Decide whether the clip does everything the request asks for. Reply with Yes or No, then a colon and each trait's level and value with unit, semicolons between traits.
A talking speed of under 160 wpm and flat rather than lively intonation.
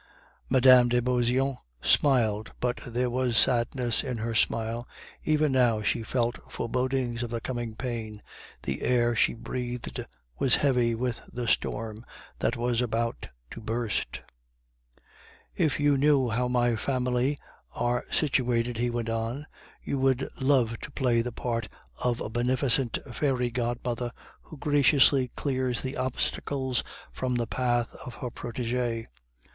Yes: average, 140 wpm; narrow, 1.7 semitones